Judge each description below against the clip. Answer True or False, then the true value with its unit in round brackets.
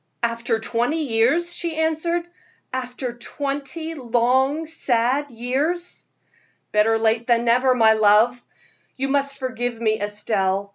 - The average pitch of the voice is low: False (245 Hz)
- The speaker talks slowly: True (115 wpm)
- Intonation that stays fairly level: False (3.9 semitones)